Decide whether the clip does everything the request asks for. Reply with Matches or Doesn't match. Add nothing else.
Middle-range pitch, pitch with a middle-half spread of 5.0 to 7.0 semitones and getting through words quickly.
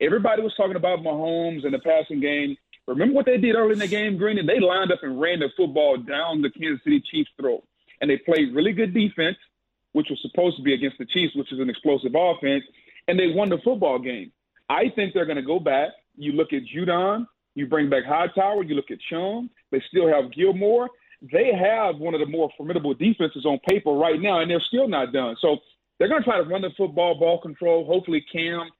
Matches